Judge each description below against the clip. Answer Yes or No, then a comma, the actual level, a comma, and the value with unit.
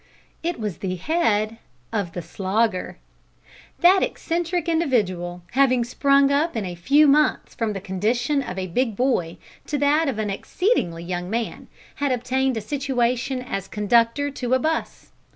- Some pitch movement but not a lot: No, wide, 6.3 semitones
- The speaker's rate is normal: Yes, average, 155 wpm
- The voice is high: Yes, high, 245 Hz